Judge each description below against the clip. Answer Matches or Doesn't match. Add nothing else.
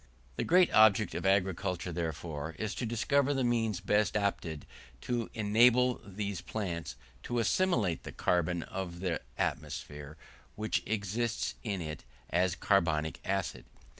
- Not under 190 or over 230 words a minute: Doesn't match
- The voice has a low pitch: Matches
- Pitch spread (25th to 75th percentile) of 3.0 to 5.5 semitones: Matches